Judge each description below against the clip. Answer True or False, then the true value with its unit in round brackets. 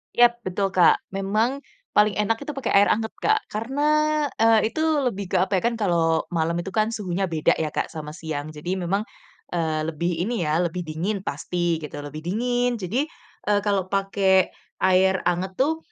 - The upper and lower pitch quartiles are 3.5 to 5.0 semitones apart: True (4.2 semitones)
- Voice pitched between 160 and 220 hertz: True (190 Hz)